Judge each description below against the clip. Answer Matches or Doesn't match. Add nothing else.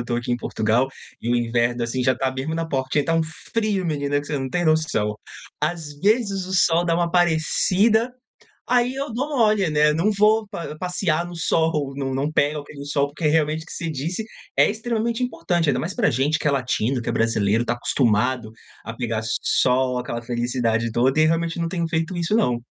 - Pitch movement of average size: Doesn't match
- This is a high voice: Doesn't match